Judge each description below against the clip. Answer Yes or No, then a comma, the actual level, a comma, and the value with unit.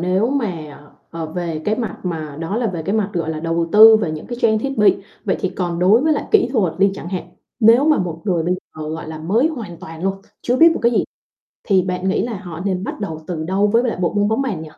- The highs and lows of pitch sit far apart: No, average, 4.9 semitones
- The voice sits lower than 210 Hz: Yes, high, 190 Hz